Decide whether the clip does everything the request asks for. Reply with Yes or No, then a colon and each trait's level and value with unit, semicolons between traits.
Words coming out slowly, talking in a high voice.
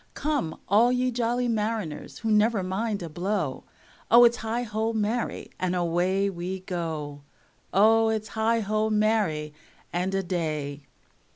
Yes: slow, 130 wpm; high, 210 Hz